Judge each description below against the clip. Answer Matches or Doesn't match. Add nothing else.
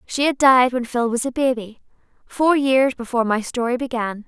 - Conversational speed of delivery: Matches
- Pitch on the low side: Doesn't match